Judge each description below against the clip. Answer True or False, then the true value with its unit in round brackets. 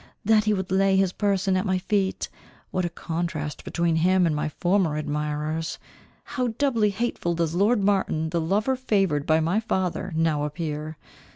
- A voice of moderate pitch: True (180 Hz)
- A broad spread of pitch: False (3.8 semitones)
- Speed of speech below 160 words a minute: False (170 wpm)